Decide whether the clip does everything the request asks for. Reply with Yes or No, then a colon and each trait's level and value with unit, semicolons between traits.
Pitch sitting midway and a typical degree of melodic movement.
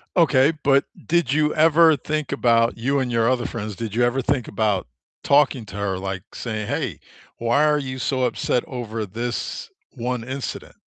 No: low, 125 Hz; average, 3.7 semitones